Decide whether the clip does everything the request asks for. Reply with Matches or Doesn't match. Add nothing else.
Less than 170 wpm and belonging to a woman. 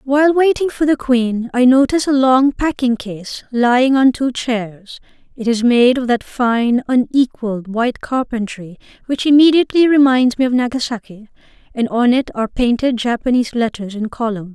Matches